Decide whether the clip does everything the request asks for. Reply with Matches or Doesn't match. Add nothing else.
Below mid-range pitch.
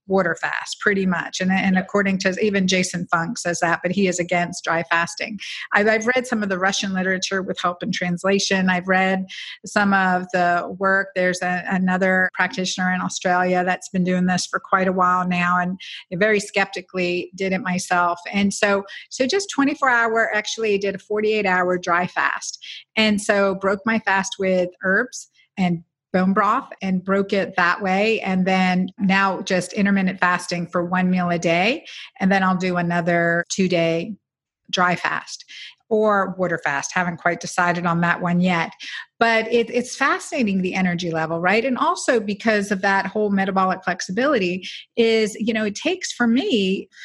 Doesn't match